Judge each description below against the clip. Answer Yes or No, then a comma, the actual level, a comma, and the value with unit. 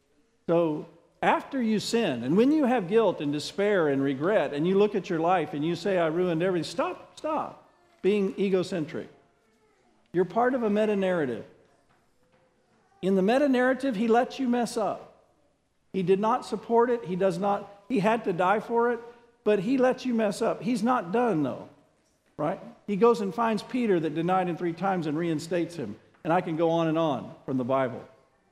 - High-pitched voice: Yes, high, 200 Hz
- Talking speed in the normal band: Yes, average, 195 wpm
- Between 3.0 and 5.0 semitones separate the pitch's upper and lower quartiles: No, wide, 5.5 semitones